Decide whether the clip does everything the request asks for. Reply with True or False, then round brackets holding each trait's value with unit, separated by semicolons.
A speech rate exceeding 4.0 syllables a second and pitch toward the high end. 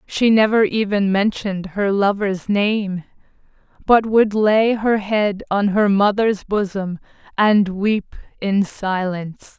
False (3.6 syllables/s; 205 Hz)